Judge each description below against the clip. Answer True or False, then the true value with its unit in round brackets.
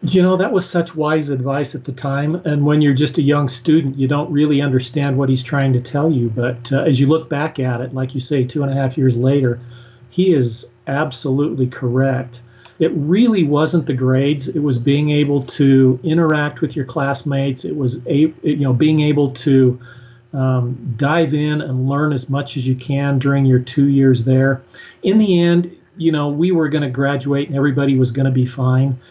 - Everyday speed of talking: False (210 wpm)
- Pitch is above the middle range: False (140 Hz)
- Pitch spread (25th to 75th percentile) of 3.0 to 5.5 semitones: False (2.5 semitones)